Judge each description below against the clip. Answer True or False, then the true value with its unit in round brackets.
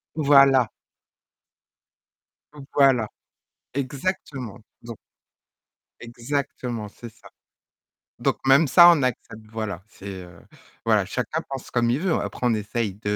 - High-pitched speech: False (120 Hz)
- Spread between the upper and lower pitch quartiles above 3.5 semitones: True (4.0 semitones)